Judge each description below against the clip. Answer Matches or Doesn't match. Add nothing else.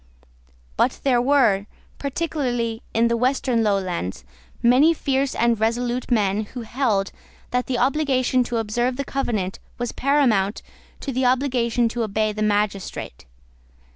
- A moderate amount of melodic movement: Matches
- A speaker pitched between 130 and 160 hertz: Doesn't match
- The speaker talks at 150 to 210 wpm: Doesn't match